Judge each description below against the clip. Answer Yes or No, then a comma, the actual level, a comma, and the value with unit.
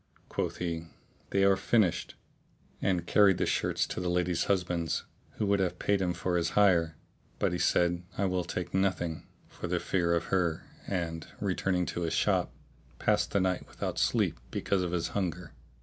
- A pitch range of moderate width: No, narrow, 2.1 semitones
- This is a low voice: Yes, very low, 90 Hz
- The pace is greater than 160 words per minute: Yes, average, 170 wpm